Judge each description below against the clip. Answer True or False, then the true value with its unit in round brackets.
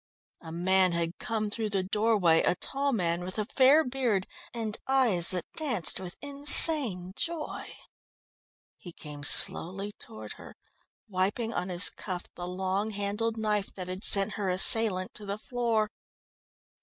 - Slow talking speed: False (150 wpm)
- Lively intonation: False (3.9 semitones)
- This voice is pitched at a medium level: False (200 Hz)